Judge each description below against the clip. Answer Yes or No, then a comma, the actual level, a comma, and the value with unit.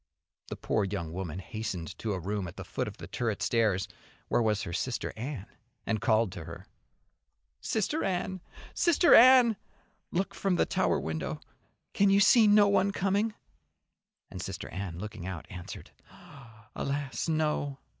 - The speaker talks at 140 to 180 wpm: Yes, average, 155 wpm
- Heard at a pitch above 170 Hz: No, low, 115 Hz